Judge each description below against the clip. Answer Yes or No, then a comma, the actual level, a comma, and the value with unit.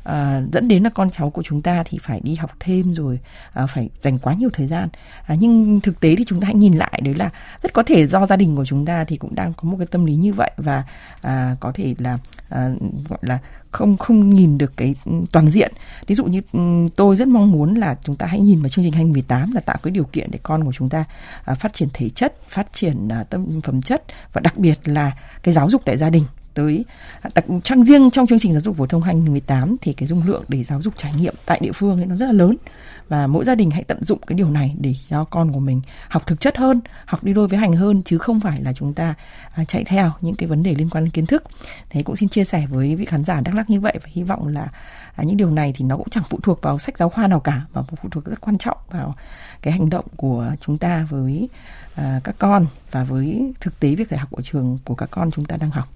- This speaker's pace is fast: Yes, fast, 270 wpm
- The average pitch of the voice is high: No, medium, 165 Hz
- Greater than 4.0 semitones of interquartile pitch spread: Yes, average, 5.1 semitones